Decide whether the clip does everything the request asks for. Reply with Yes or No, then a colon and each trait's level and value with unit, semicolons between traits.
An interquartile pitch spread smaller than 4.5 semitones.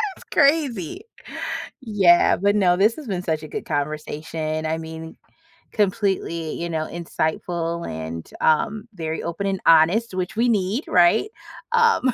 No: average, 4.8 semitones